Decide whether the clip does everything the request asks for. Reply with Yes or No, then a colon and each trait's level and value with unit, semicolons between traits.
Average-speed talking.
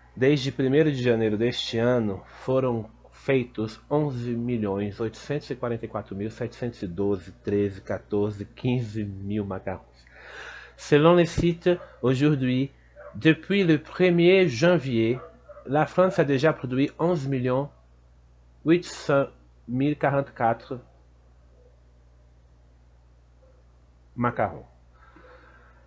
No: slow, 65 wpm